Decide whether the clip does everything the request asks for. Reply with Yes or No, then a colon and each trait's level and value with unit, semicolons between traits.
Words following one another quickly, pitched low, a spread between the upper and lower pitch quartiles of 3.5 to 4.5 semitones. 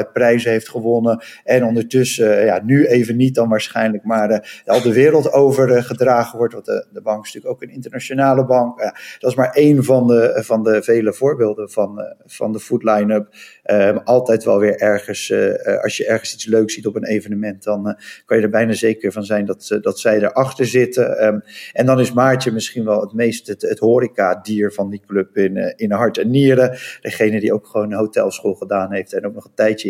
No: fast, 215 wpm; low, 115 Hz; average, 2.9 semitones